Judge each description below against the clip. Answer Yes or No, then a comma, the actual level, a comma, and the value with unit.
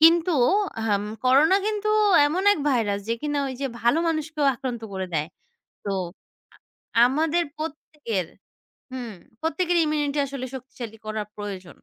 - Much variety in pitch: Yes, wide, 5.8 semitones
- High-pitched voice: Yes, very high, 275 Hz